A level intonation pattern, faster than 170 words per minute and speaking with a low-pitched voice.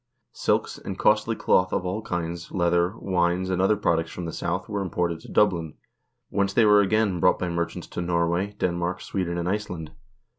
Yes: narrow, 2.2 semitones; average, 185 wpm; very low, 90 Hz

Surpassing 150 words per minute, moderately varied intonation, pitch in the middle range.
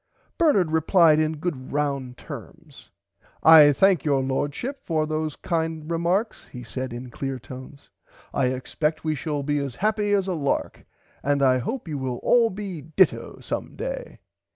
Yes: average, 160 wpm; average, 4.9 semitones; medium, 155 Hz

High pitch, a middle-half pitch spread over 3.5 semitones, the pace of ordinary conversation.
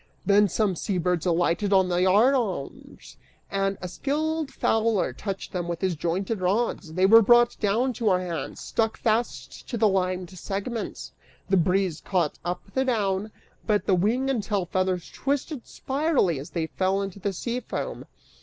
Yes: high, 195 Hz; average, 3.9 semitones; average, 175 wpm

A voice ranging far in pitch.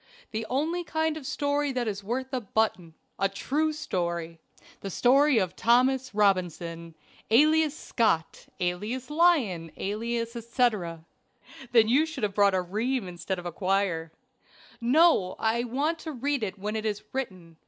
Yes: wide, 6.3 semitones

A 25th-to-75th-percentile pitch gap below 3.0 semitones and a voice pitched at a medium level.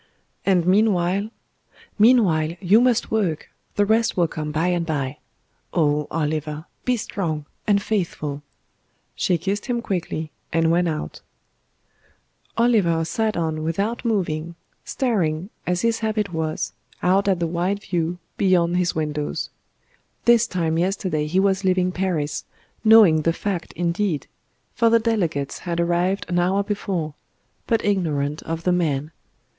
No: average, 4.1 semitones; medium, 175 Hz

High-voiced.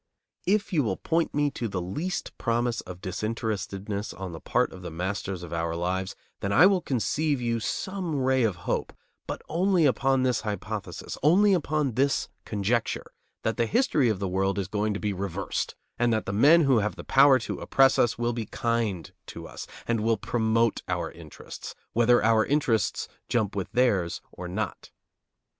No: low, 115 Hz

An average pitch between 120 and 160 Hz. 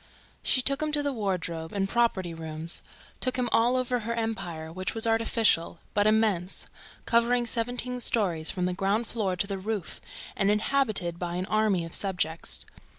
No: high, 210 Hz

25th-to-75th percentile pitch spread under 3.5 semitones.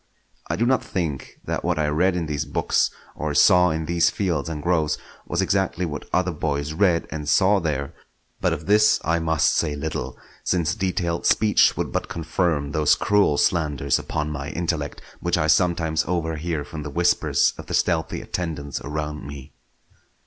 Yes: average, 2.9 semitones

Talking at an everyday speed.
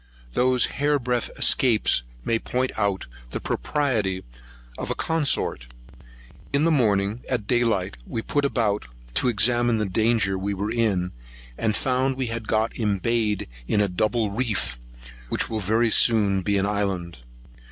Yes: average, 150 wpm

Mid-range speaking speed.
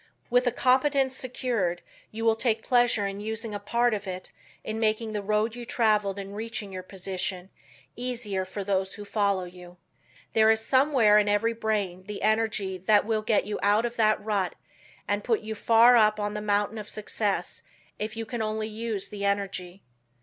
Yes: average, 185 wpm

